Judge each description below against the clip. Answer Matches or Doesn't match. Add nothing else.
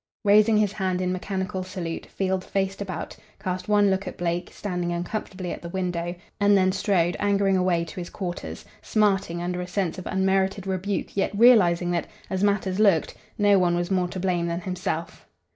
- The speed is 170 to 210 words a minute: Matches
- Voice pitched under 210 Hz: Matches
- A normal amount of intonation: Doesn't match